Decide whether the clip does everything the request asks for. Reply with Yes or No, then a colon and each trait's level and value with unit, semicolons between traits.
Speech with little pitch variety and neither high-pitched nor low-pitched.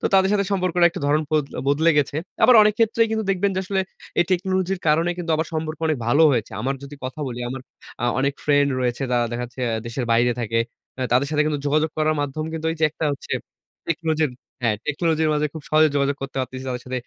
No: average, 4.0 semitones; medium, 150 Hz